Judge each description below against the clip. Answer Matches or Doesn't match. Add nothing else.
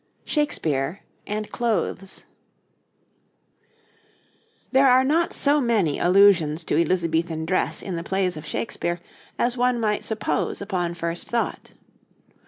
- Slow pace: Matches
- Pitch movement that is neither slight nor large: Doesn't match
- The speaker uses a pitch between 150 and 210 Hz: Matches